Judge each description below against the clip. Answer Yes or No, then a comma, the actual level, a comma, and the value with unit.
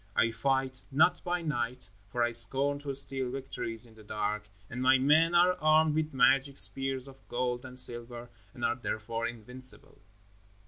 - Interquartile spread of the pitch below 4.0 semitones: Yes, average, 2.8 semitones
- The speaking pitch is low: Yes, low, 130 Hz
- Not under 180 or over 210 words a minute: No, average, 170 wpm